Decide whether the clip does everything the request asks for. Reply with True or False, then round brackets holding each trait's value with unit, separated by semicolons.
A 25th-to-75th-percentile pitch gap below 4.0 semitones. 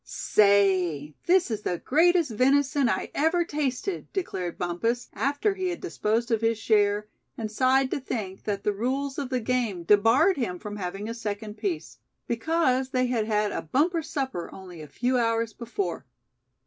False (5.2 semitones)